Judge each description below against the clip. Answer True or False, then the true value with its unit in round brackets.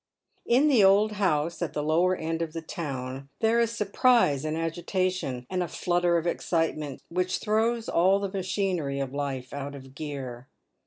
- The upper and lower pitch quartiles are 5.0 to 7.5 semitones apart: True (5.4 semitones)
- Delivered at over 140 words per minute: True (170 wpm)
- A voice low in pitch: False (170 Hz)